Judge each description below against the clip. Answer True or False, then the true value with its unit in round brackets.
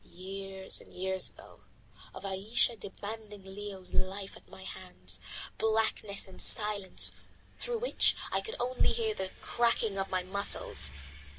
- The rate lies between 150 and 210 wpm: False (135 wpm)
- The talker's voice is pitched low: False (195 Hz)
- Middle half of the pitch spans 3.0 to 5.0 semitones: False (2.6 semitones)